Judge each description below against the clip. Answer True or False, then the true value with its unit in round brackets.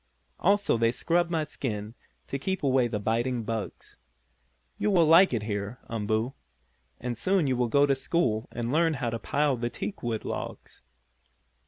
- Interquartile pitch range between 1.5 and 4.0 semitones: False (5.4 semitones)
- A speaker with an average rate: True (165 wpm)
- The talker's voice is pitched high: False (125 Hz)